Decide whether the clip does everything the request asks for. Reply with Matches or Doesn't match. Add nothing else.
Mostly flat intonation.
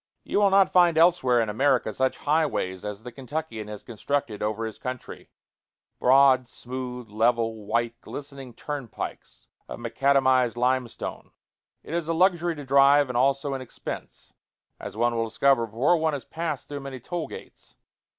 Doesn't match